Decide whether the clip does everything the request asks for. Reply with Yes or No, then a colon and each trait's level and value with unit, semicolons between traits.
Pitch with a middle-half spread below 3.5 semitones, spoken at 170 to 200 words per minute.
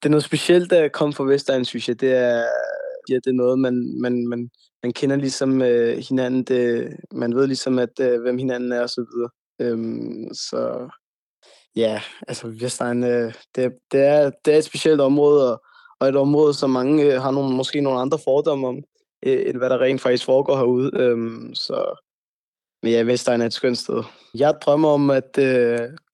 Yes: average, 2.7 semitones; average, 195 wpm